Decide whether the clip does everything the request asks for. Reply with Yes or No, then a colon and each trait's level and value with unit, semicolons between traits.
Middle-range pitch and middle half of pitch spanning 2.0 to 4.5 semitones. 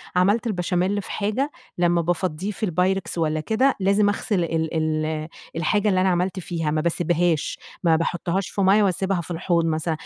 Yes: medium, 175 Hz; average, 3.1 semitones